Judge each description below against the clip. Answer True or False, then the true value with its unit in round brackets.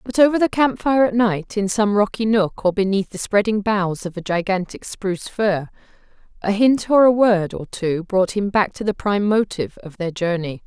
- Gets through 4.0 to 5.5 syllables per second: True (5.0 syllables/s)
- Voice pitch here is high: True (200 Hz)